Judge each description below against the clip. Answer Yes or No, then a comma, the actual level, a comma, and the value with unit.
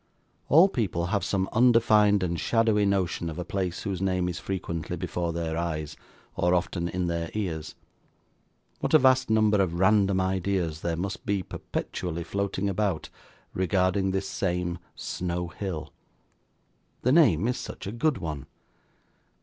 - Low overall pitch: Yes, very low, 95 Hz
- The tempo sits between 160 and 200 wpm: No, average, 150 wpm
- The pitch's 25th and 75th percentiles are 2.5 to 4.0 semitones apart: Yes, average, 3.0 semitones